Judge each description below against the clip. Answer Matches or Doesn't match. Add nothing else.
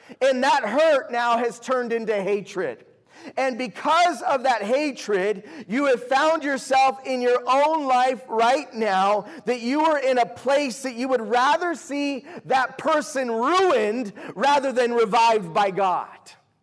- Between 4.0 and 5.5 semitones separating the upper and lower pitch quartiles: Doesn't match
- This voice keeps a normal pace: Matches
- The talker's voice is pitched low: Doesn't match